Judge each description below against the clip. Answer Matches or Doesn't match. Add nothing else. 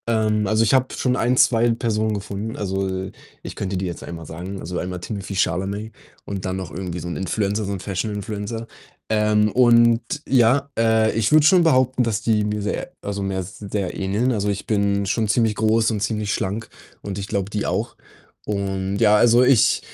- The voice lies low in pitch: Matches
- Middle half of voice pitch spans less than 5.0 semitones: Matches